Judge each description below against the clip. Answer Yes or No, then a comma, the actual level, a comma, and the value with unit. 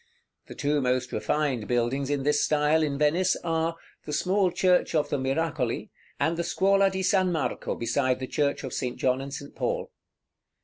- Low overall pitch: No, medium, 150 Hz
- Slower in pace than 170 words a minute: No, average, 180 wpm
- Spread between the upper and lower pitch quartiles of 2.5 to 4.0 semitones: No, average, 4.4 semitones